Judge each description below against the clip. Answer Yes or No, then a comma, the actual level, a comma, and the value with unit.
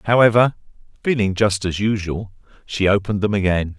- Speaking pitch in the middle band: No, low, 100 Hz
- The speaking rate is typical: Yes, average, 145 wpm